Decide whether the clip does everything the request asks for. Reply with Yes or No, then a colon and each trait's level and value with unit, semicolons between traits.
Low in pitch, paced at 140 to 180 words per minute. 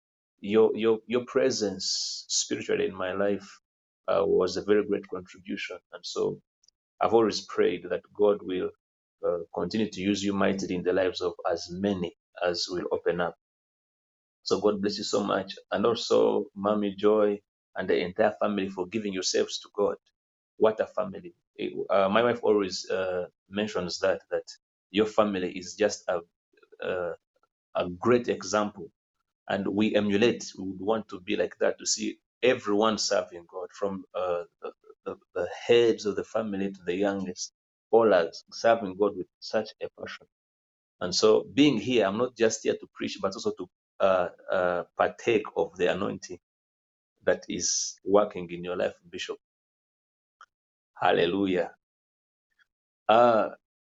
Yes: low, 105 Hz; average, 155 wpm